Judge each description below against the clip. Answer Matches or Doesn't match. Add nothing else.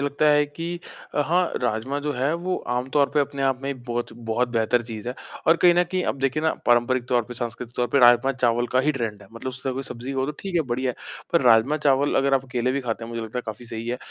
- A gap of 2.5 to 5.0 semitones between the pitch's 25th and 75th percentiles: Matches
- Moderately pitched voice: Doesn't match